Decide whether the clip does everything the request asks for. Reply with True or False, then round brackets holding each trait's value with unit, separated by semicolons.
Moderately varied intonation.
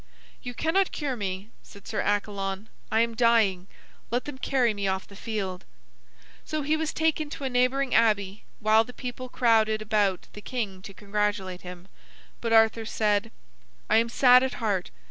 True (3.7 semitones)